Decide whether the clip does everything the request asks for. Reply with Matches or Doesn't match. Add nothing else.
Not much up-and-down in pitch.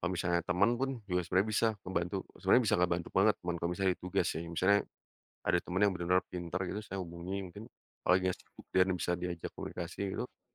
Matches